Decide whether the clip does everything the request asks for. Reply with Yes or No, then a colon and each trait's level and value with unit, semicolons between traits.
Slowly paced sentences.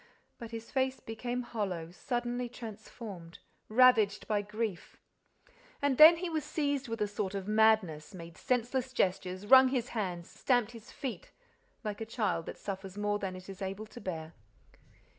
No: average, 160 wpm